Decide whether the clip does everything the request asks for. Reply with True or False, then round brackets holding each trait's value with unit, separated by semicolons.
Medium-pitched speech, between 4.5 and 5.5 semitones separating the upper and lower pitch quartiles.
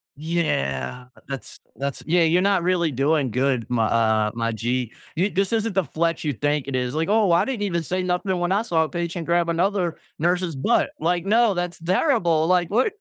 True (170 Hz; 5.0 semitones)